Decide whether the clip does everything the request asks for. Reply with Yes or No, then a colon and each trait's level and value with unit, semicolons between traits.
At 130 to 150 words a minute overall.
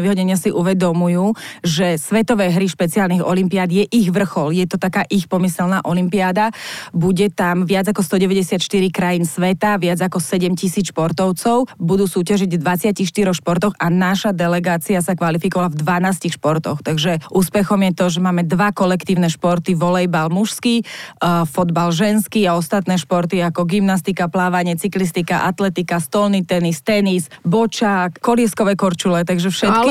Yes: average, 140 wpm